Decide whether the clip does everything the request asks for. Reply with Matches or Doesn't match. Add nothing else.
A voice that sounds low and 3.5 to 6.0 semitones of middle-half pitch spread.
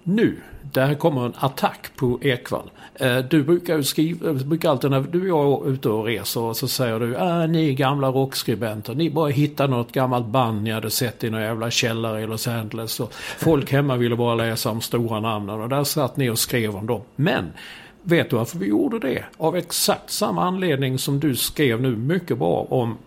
Matches